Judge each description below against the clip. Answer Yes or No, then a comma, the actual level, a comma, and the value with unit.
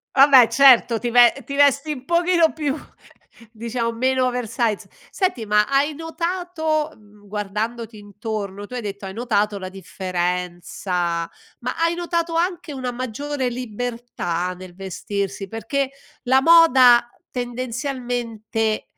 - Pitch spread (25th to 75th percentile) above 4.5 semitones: Yes, average, 5.2 semitones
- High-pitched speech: Yes, high, 240 Hz